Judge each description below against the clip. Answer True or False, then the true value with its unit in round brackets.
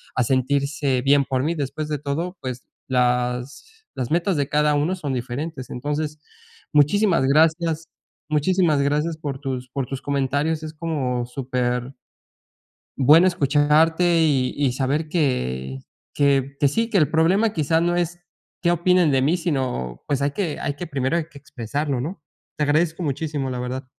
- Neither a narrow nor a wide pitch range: True (3.6 semitones)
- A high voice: False (145 Hz)